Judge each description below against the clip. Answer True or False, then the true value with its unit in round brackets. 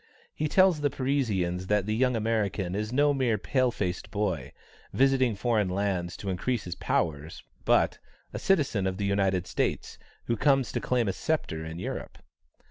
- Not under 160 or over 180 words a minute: True (170 wpm)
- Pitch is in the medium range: False (105 Hz)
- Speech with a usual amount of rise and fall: False (5.7 semitones)